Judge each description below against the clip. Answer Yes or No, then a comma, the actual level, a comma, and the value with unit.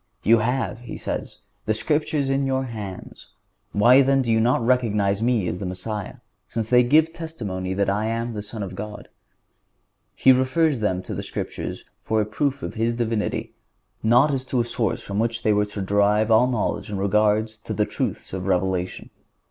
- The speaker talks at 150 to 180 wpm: No, average, 190 wpm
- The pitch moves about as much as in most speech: Yes, average, 3.5 semitones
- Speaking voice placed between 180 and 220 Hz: No, low, 110 Hz